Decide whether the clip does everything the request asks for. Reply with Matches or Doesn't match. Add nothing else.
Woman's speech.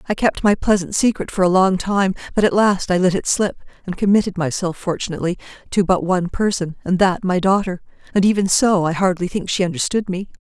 Matches